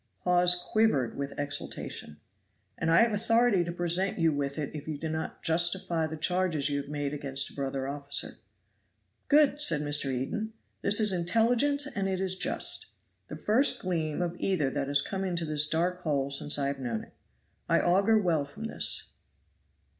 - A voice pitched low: No, medium, 165 Hz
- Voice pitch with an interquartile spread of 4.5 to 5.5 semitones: Yes, average, 5.0 semitones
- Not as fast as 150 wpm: No, average, 180 wpm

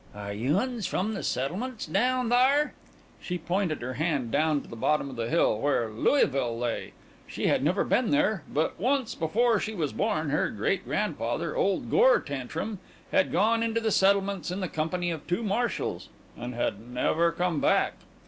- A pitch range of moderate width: No, wide, 7.8 semitones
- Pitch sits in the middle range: Yes, medium, 175 Hz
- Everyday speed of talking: Yes, average, 180 wpm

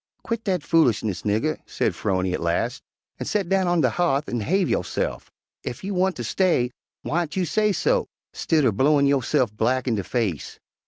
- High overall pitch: No, medium, 145 Hz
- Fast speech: No, average, 170 wpm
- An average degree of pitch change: No, wide, 8.1 semitones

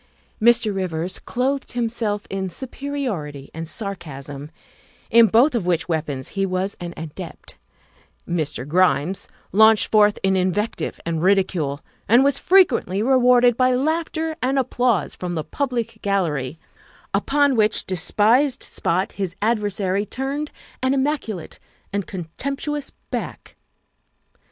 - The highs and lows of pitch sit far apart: Yes, wide, 6.3 semitones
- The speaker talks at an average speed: No, slow, 125 wpm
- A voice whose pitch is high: Yes, high, 205 Hz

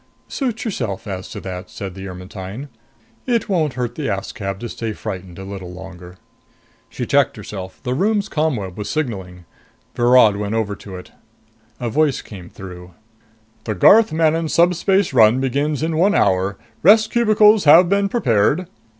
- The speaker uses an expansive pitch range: Yes, wide, 9.0 semitones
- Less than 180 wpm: Yes, average, 160 wpm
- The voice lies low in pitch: Yes, low, 115 Hz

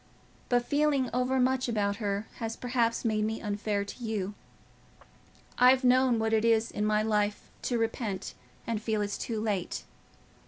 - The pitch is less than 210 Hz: No, high, 225 Hz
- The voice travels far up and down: No, average, 2.8 semitones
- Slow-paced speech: No, average, 155 wpm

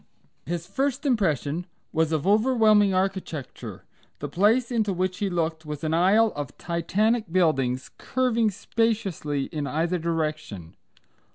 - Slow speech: Yes, slow, 125 wpm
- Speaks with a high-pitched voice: No, medium, 180 Hz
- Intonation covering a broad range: Yes, wide, 5.7 semitones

